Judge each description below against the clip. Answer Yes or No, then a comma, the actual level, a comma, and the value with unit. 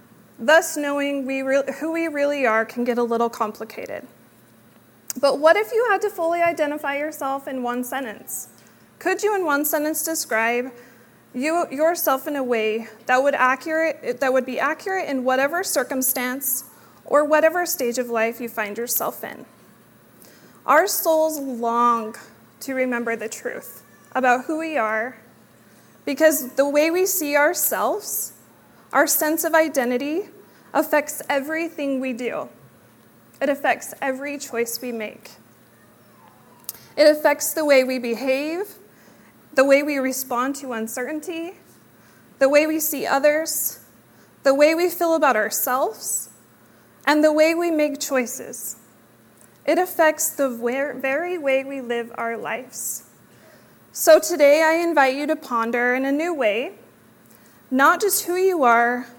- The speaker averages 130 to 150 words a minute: Yes, average, 140 wpm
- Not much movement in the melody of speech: No, average, 4.3 semitones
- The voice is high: Yes, very high, 275 Hz